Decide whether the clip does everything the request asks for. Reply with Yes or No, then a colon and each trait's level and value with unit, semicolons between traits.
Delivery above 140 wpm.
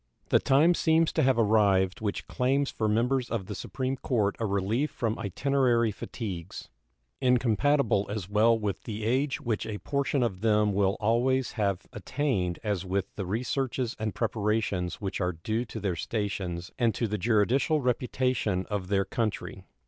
Yes: average, 165 wpm